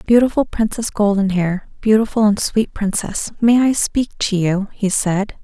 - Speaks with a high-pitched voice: Yes, high, 210 Hz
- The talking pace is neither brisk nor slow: Yes, average, 155 wpm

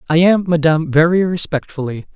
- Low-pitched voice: No, medium, 160 Hz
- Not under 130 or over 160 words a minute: Yes, average, 140 wpm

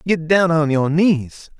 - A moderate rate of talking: Yes, average, 190 wpm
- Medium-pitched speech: Yes, medium, 160 Hz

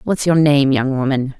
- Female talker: Yes, female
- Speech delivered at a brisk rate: Yes, fast, 215 wpm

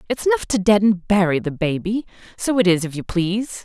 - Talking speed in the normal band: No, fast, 230 wpm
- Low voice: No, high, 195 Hz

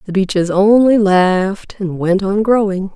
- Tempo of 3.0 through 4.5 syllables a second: Yes, 4.3 syllables/s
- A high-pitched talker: Yes, high, 195 Hz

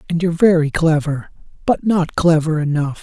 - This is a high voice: No, medium, 160 Hz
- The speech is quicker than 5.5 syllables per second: No, 5.2 syllables/s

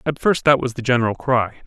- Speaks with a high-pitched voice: No, low, 125 Hz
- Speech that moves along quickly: Yes, fast, 255 wpm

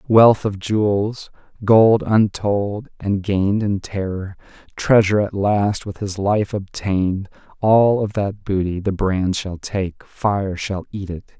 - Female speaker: No, male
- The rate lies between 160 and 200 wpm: No, average, 145 wpm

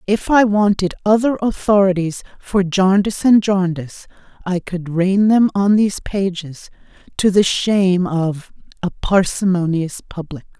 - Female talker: Yes, female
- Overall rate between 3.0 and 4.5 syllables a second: Yes, 4.4 syllables/s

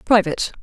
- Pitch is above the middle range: Yes, high, 205 Hz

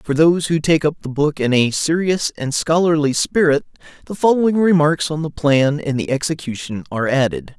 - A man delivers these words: Yes, male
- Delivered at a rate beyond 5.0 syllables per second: Yes, 5.3 syllables/s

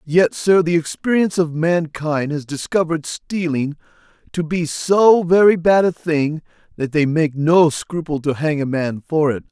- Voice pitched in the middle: Yes, medium, 160 Hz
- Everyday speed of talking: Yes, average, 170 wpm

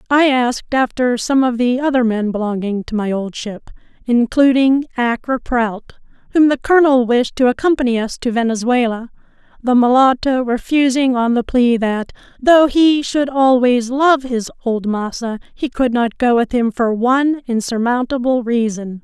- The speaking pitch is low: No, high, 245 Hz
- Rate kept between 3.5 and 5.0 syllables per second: Yes, 4.6 syllables/s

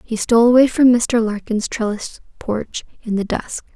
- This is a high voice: Yes, high, 230 Hz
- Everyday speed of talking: Yes, average, 175 wpm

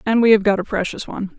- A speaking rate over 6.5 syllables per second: Yes, 7.1 syllables/s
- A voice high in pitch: Yes, high, 210 Hz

